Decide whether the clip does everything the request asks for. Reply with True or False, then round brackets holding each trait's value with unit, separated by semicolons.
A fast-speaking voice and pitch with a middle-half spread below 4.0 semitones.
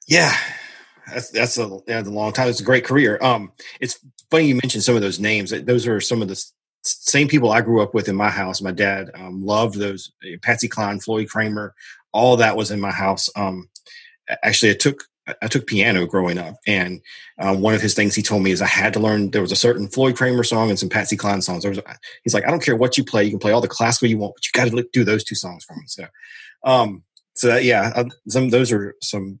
True (250 wpm; 3.5 semitones)